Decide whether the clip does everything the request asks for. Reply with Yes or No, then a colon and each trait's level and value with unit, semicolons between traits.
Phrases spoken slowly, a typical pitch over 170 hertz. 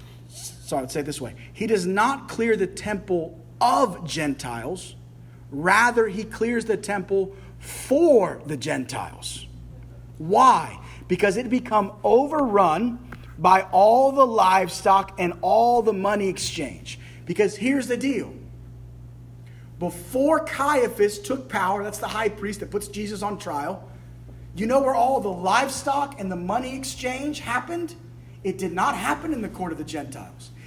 No: average, 145 wpm; high, 190 Hz